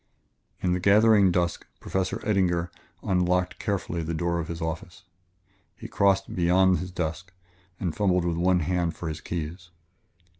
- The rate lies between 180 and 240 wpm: No, average, 155 wpm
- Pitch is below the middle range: Yes, very low, 90 Hz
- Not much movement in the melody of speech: Yes, narrow, 1.7 semitones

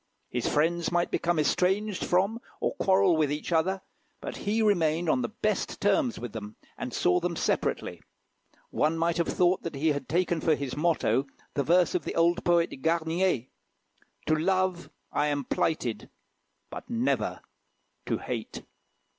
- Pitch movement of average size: Yes, average, 3.5 semitones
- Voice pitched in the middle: Yes, medium, 170 Hz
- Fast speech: No, average, 165 wpm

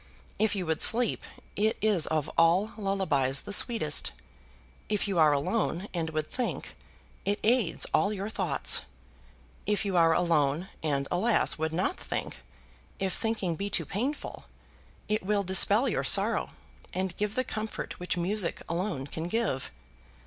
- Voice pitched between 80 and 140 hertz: No, high, 190 Hz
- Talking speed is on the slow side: No, average, 150 wpm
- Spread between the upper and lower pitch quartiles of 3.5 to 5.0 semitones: Yes, average, 4.6 semitones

